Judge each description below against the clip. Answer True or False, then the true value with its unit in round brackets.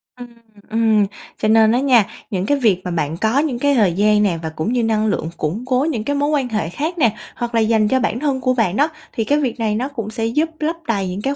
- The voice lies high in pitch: True (230 Hz)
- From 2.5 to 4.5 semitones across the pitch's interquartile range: True (3.9 semitones)